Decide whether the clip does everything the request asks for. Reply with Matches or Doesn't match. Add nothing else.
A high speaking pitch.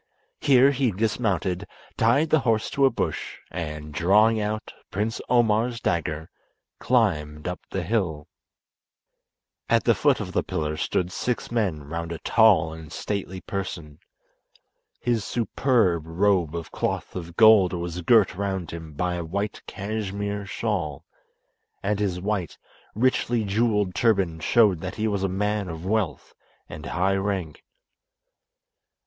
Doesn't match